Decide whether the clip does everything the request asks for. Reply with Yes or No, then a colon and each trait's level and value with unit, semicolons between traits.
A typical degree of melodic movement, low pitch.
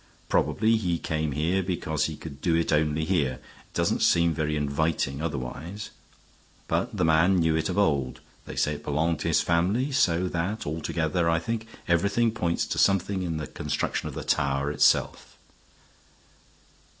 Yes: average, 3.3 semitones; very low, 85 Hz